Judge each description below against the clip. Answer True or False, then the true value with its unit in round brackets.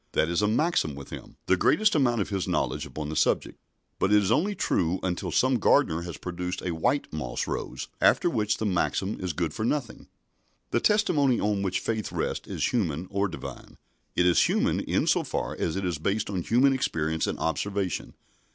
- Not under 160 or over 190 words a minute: False (200 wpm)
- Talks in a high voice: False (100 Hz)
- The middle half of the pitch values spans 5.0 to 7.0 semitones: True (5.6 semitones)